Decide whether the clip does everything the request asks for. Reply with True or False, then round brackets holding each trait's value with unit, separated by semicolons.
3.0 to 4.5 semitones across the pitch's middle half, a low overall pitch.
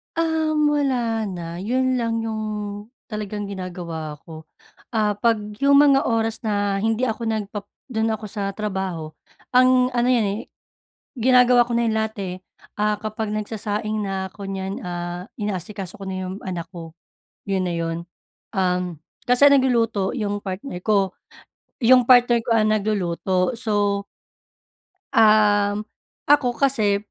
False (3.7 semitones; 210 Hz)